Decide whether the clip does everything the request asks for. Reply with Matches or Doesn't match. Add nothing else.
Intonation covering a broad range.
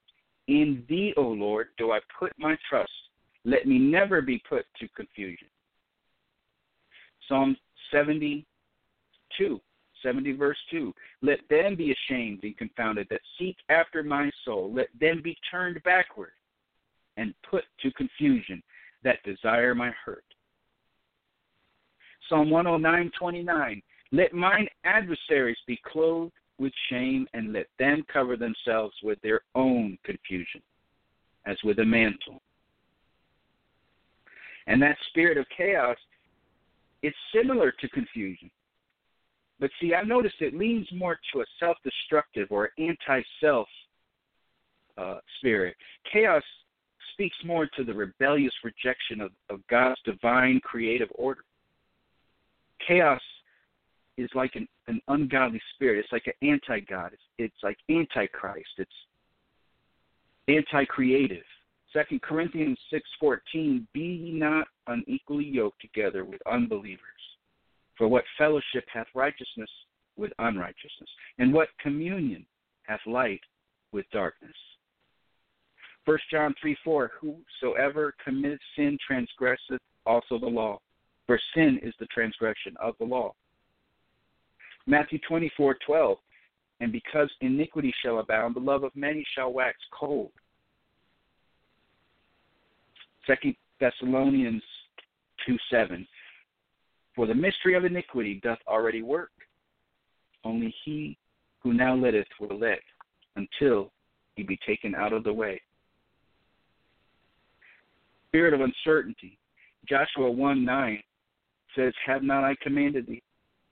Matches